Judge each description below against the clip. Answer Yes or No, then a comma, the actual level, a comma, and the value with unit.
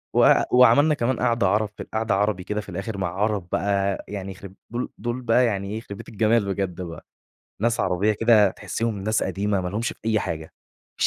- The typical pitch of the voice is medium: No, low, 105 Hz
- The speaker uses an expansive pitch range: No, average, 2.8 semitones